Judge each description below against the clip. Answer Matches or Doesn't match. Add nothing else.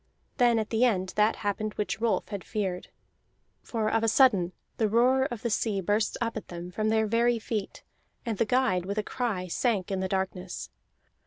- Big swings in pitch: Doesn't match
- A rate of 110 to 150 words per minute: Doesn't match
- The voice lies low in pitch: Doesn't match